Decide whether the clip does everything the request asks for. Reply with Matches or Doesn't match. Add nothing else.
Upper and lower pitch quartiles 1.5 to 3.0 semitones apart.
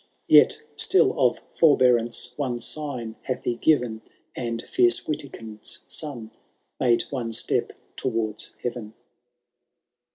Doesn't match